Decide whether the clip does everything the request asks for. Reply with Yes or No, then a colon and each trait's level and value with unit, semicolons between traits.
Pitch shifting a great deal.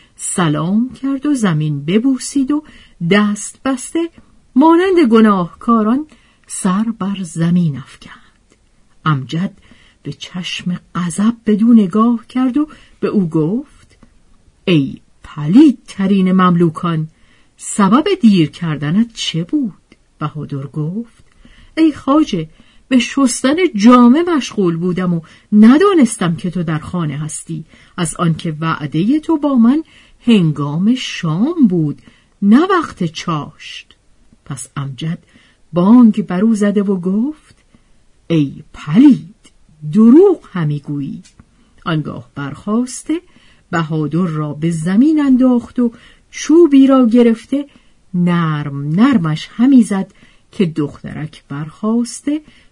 Yes: wide, 7.4 semitones